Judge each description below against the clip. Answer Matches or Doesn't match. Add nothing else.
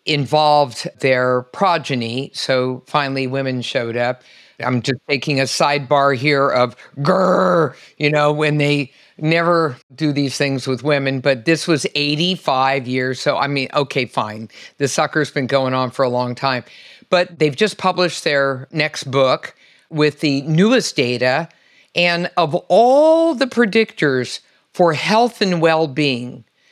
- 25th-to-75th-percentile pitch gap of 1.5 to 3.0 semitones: Doesn't match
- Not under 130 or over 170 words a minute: Matches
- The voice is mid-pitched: Matches